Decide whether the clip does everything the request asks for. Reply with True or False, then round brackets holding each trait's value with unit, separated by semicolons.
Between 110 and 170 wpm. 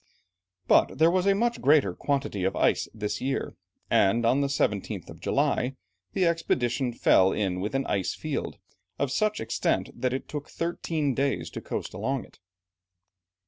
True (160 wpm)